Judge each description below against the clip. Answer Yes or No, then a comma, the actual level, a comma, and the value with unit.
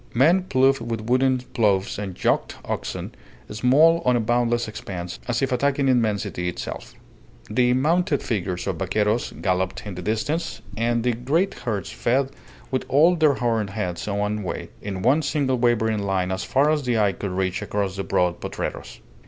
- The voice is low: Yes, low, 115 Hz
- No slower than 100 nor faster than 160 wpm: No, average, 170 wpm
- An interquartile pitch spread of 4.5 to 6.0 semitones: Yes, average, 4.9 semitones